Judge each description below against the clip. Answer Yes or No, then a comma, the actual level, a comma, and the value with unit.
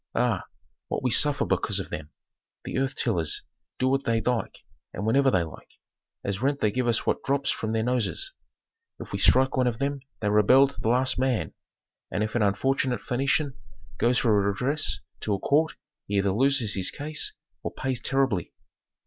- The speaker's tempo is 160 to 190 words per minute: Yes, average, 185 wpm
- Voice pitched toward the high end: No, low, 125 Hz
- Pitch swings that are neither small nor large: Yes, average, 4.2 semitones